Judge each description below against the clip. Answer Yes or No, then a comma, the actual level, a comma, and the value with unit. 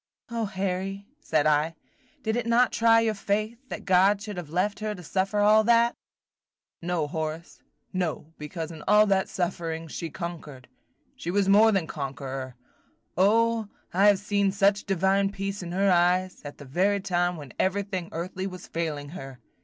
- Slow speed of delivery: No, average, 170 wpm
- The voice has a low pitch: No, high, 190 Hz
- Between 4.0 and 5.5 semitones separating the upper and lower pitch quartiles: No, average, 3.6 semitones